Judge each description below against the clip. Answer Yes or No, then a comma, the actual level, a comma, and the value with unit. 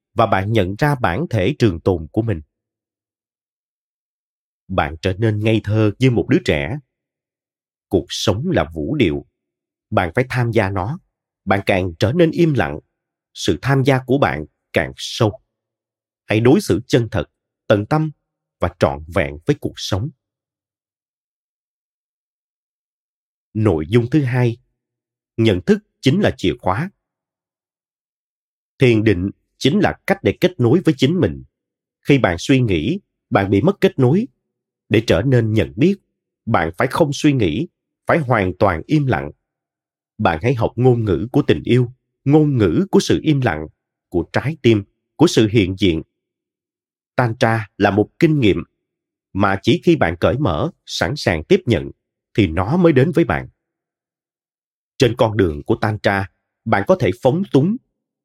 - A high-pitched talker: No, low, 115 Hz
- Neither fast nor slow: No, slow, 160 wpm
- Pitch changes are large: Yes, wide, 6.0 semitones